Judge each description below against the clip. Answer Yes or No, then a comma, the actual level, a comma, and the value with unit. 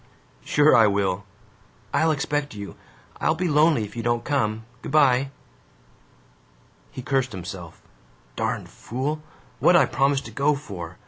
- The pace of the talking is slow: No, average, 145 wpm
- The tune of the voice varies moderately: No, wide, 5.9 semitones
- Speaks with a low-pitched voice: Yes, low, 130 Hz